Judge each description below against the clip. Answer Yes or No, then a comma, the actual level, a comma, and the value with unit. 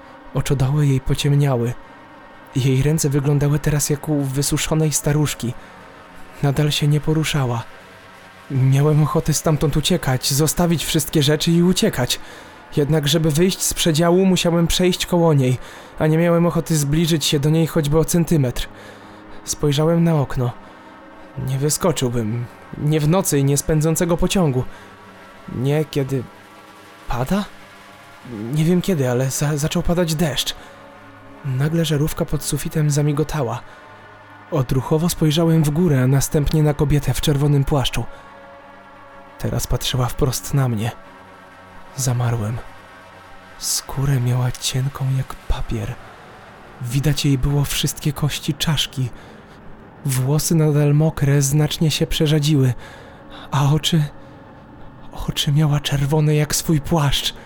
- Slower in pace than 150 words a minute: Yes, average, 120 wpm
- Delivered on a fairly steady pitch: No, average, 3.8 semitones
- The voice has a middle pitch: Yes, medium, 145 Hz